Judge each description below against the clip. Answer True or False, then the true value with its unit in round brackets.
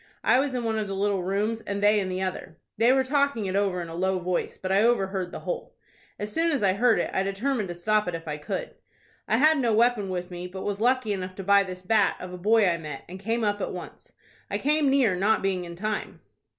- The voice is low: False (200 Hz)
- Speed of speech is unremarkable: False (260 wpm)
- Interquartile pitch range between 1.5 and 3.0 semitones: False (3.7 semitones)